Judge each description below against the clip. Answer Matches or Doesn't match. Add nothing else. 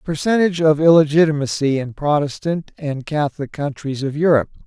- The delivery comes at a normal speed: Doesn't match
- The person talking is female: Doesn't match